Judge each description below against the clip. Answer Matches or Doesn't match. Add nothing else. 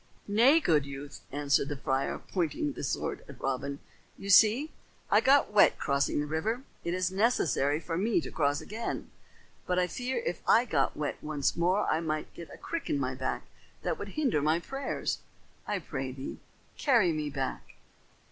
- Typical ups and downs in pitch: Doesn't match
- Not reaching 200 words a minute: Matches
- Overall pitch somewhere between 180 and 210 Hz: Doesn't match